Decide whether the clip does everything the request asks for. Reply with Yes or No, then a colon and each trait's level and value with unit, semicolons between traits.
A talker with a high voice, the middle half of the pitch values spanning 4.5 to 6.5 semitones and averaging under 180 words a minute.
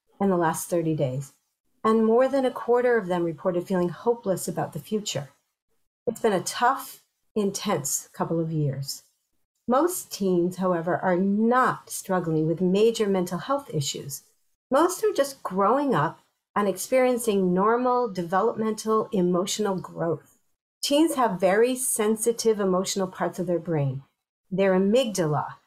Yes: high, 195 Hz; average, 4.9 semitones; average, 140 wpm